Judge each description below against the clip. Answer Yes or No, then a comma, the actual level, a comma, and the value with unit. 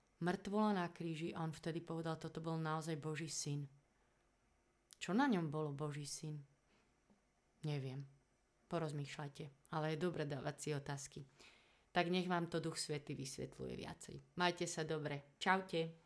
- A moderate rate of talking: Yes, average, 140 wpm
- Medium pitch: Yes, medium, 160 Hz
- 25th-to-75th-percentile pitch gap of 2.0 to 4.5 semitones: Yes, narrow, 2.6 semitones